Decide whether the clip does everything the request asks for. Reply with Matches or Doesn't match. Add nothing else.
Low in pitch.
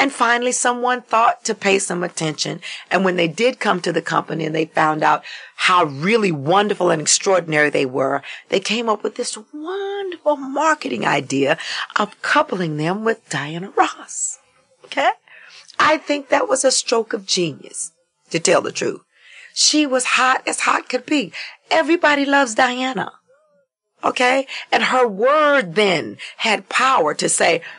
Doesn't match